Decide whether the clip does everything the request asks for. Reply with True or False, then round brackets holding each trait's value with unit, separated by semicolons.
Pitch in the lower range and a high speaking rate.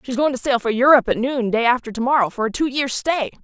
False (250 Hz; 295 wpm)